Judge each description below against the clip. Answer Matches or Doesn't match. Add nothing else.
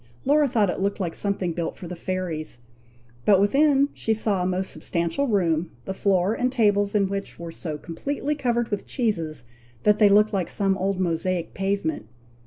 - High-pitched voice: Matches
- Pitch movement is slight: Doesn't match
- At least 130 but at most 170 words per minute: Doesn't match